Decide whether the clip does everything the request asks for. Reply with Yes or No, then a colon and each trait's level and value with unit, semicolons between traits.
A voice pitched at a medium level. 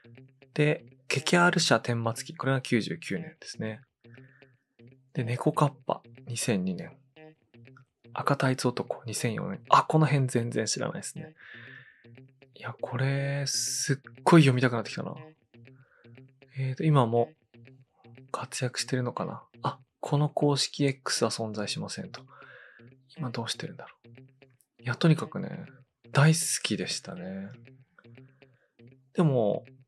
No: low, 130 Hz